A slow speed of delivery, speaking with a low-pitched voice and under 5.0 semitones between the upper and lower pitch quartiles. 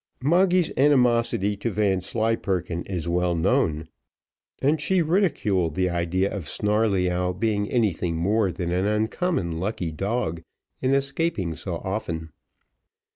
No: slow, 120 wpm; low, 100 Hz; wide, 5.6 semitones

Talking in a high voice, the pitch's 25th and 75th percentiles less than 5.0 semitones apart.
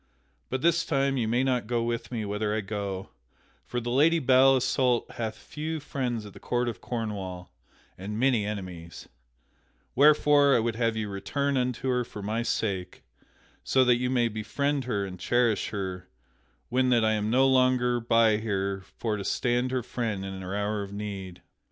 No: low, 115 Hz; average, 3.7 semitones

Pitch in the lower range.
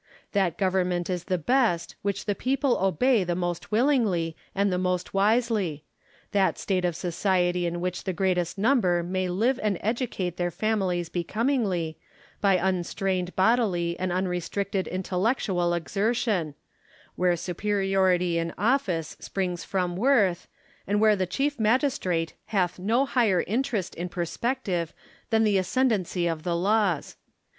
No: medium, 185 Hz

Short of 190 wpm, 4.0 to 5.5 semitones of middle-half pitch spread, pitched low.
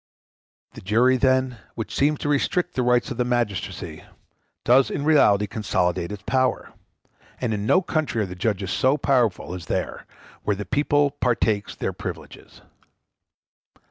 Yes: average, 150 wpm; average, 4.8 semitones; low, 120 Hz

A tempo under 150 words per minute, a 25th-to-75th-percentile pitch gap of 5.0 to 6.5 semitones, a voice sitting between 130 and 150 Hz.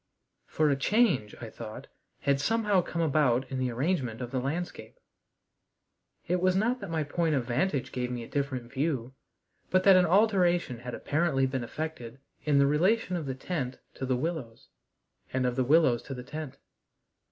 No: average, 180 wpm; wide, 5.5 semitones; medium, 140 Hz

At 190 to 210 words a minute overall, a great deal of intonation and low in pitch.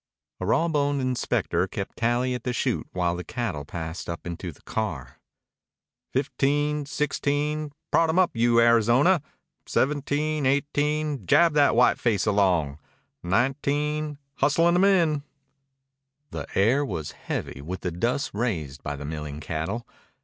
No: slow, 135 wpm; wide, 8.6 semitones; low, 125 Hz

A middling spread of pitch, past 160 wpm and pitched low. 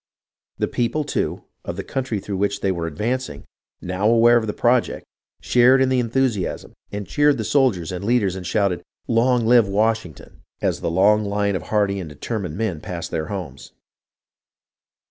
Yes: average, 4.3 semitones; average, 175 wpm; low, 105 Hz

